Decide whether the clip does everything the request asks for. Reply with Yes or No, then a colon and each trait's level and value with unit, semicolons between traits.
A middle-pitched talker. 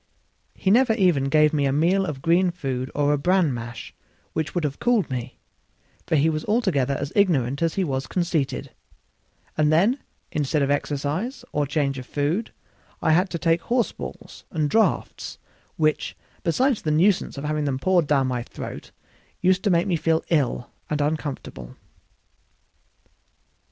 Yes: medium, 155 Hz